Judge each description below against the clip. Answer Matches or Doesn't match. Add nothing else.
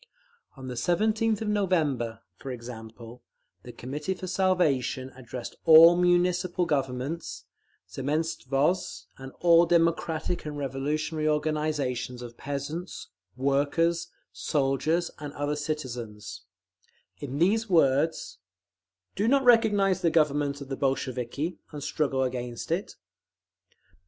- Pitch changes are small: Doesn't match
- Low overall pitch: Doesn't match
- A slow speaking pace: Matches